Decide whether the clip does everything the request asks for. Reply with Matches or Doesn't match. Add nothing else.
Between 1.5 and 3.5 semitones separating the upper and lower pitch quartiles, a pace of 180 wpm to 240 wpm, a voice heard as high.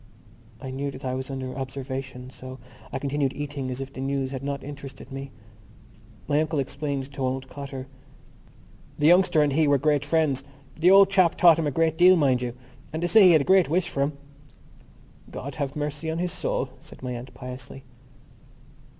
Doesn't match